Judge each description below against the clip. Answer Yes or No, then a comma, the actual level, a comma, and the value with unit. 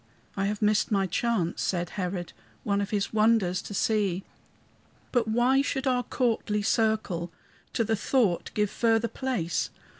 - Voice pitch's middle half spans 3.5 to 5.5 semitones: No, average, 3.1 semitones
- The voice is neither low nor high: No, high, 210 Hz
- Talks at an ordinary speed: Yes, average, 150 wpm